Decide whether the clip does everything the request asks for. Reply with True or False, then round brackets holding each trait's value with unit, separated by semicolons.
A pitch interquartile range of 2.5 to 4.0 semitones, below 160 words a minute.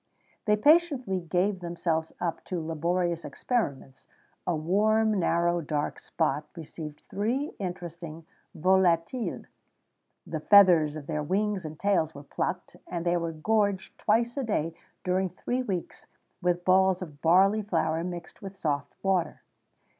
True (3.7 semitones; 135 wpm)